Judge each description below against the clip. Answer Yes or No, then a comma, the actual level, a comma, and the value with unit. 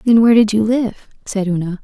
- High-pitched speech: Yes, high, 215 Hz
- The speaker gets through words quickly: Yes, fast, 230 wpm